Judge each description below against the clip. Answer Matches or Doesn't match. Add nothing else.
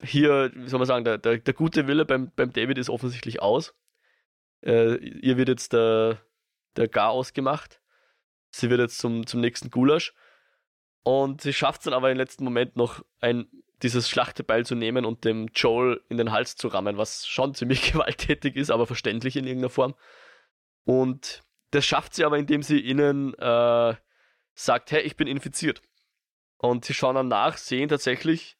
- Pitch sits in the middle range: Doesn't match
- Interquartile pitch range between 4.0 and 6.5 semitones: Doesn't match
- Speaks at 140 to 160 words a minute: Doesn't match